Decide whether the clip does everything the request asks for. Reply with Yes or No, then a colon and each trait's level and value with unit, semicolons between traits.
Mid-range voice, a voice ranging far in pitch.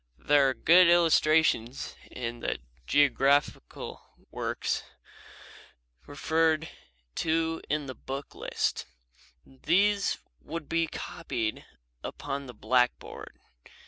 No: medium, 145 Hz; average, 3.7 semitones